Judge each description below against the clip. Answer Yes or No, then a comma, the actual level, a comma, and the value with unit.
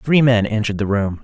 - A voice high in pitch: No, low, 110 Hz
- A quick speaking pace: Yes, fast, 245 wpm